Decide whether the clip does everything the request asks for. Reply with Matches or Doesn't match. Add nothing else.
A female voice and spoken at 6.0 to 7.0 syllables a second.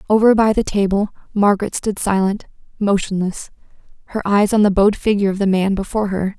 Matches